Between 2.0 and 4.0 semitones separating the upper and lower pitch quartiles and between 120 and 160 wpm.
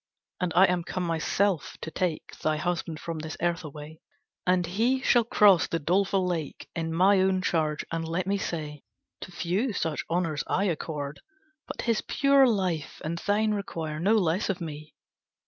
No: average, 3.4 semitones; average, 175 wpm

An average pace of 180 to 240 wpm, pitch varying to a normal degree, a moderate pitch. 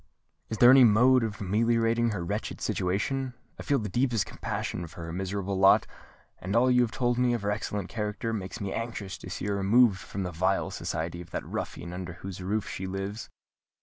No: fast, 205 wpm; average, 3.8 semitones; low, 105 Hz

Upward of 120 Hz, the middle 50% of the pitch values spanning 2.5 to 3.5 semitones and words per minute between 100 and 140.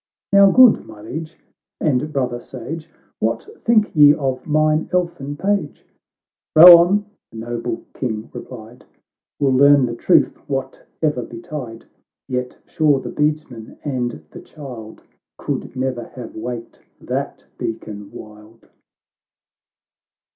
No: low, 135 Hz; average, 4.6 semitones; slow, 135 wpm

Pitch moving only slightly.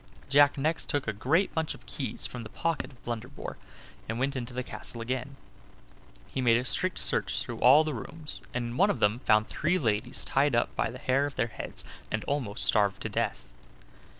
No: average, 3.9 semitones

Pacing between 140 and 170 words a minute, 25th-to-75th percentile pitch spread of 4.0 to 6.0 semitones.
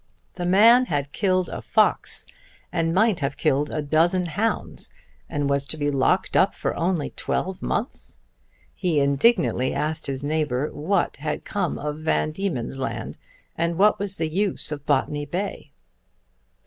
Yes: average, 155 wpm; average, 4.4 semitones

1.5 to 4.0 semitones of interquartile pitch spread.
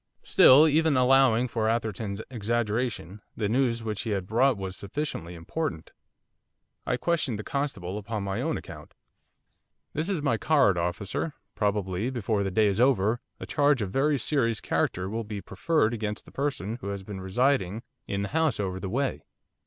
No: average, 5.1 semitones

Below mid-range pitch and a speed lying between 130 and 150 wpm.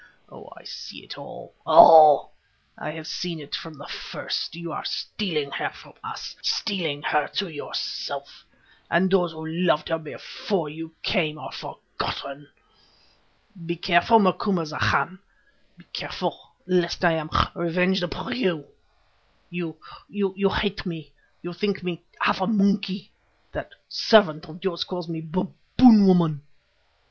No: medium, 170 Hz; slow, 135 wpm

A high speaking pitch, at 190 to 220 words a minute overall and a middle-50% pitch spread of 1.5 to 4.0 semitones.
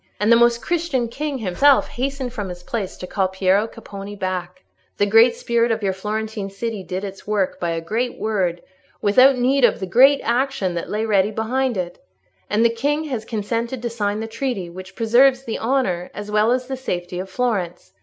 No: high, 220 Hz; average, 200 wpm; average, 4.4 semitones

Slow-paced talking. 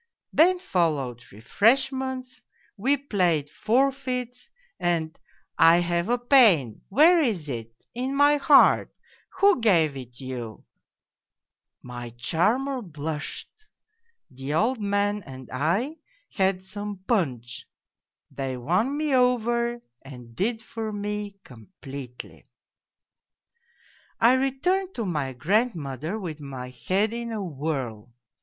Yes: slow, 130 wpm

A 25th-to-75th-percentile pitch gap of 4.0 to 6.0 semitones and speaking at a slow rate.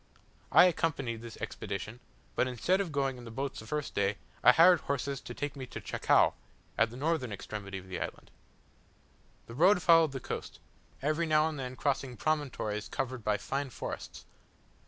No: average, 5.1 semitones; average, 175 wpm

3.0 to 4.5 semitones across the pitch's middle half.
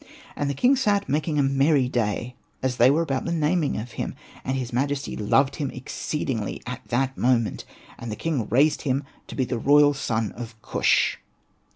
Yes: average, 3.3 semitones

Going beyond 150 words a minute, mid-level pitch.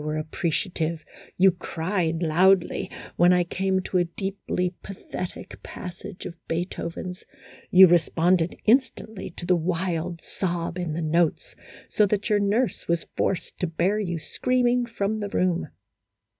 No: average, 145 wpm; medium, 180 Hz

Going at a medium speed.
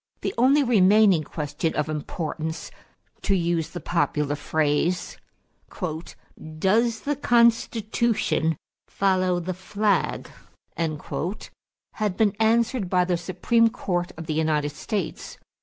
No: slow, 110 wpm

